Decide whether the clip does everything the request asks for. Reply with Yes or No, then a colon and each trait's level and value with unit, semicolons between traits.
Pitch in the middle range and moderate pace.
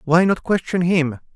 Yes: medium, 170 Hz; average, 175 wpm